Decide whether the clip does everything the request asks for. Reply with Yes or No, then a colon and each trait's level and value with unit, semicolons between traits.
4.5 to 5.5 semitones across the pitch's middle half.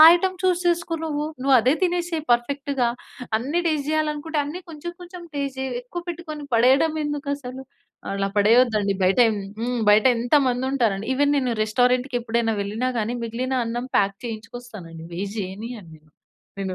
Yes: average, 4.8 semitones